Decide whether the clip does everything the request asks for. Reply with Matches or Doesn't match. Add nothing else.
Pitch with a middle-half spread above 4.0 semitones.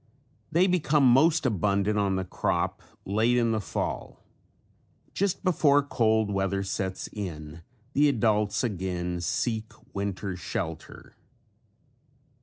Matches